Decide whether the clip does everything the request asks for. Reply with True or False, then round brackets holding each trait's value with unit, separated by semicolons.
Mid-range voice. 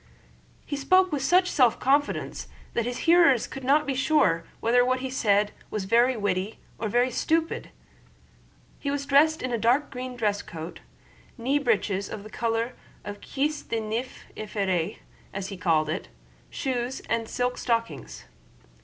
False (245 Hz)